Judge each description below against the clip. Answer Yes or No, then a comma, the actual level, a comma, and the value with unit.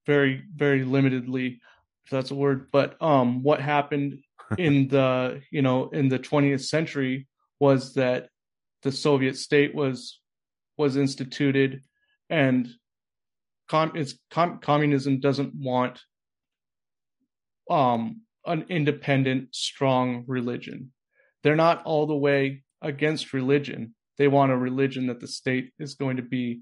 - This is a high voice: No, medium, 140 Hz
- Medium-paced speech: No, slow, 130 wpm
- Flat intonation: Yes, narrow, 2.1 semitones